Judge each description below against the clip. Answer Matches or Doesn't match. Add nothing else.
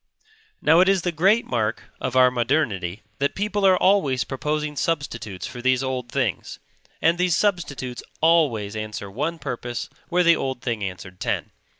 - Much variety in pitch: Matches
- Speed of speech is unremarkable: Matches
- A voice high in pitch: Doesn't match